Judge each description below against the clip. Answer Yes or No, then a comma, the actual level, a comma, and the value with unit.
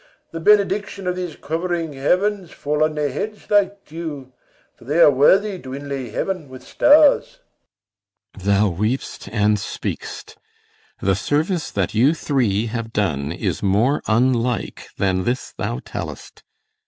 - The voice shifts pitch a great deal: Yes, wide, 8.4 semitones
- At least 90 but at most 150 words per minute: Yes, average, 140 wpm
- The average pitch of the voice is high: No, medium, 140 Hz